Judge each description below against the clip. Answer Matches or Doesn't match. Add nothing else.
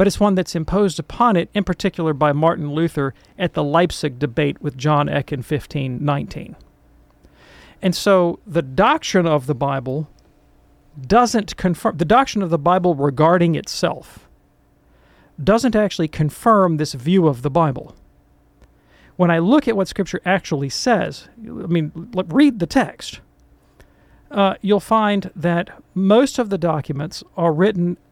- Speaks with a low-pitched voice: Doesn't match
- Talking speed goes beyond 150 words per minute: Doesn't match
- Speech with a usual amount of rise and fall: Matches